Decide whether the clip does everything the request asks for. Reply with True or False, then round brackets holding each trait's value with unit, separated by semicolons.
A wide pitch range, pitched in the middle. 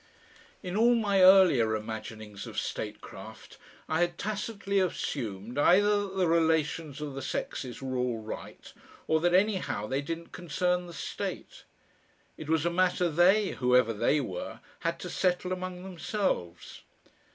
True (6.5 semitones; 165 Hz)